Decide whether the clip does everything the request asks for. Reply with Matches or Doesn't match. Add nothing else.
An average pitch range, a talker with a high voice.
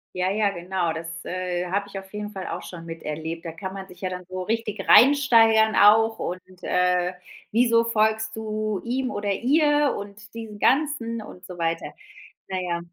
Matches